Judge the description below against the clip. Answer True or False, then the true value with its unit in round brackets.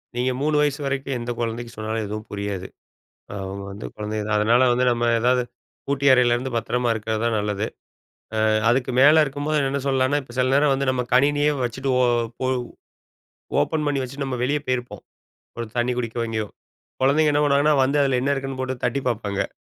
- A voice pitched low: True (125 Hz)